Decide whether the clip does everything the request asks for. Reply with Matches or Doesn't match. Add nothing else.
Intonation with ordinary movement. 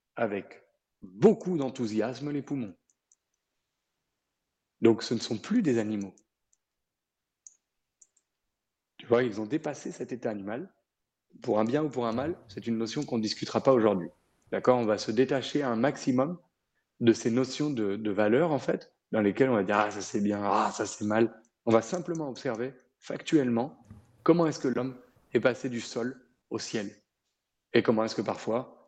Matches